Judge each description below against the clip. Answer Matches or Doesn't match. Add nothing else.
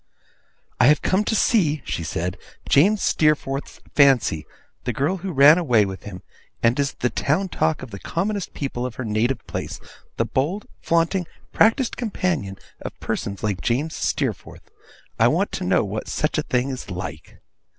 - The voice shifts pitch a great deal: Matches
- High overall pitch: Doesn't match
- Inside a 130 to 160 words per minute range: Doesn't match